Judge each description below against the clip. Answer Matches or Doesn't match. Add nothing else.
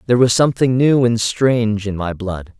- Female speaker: Doesn't match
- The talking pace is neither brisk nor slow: Doesn't match